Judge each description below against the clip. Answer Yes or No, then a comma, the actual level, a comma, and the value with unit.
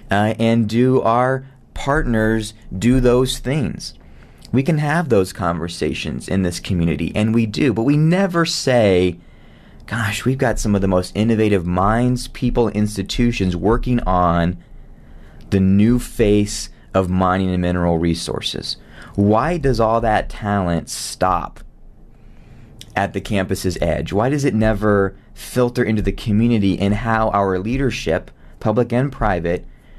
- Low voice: Yes, low, 105 Hz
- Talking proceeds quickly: No, average, 140 wpm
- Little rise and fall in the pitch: No, average, 4.6 semitones